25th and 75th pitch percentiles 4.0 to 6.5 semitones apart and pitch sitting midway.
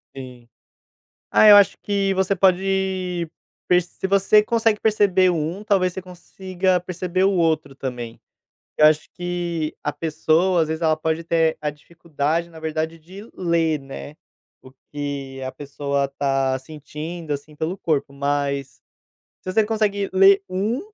Yes: average, 4.3 semitones; medium, 170 Hz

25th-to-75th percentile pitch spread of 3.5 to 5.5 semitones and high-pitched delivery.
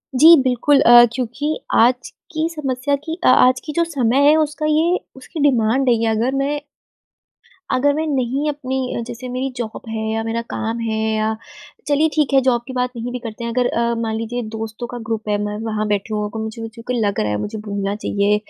Yes: average, 3.9 semitones; high, 245 Hz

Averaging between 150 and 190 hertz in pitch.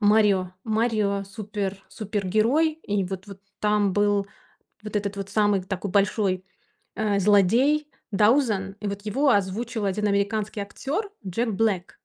No: high, 205 Hz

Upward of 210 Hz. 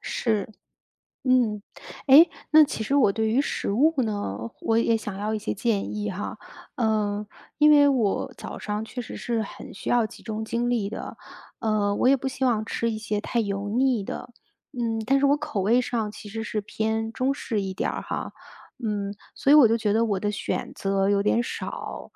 Yes: high, 220 Hz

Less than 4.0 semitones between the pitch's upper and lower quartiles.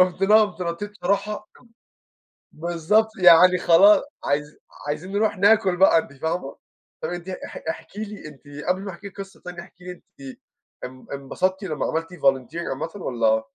No: average, 4.3 semitones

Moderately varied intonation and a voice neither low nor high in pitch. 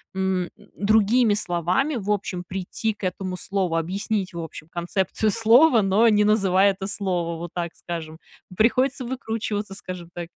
No: average, 3.5 semitones; high, 195 Hz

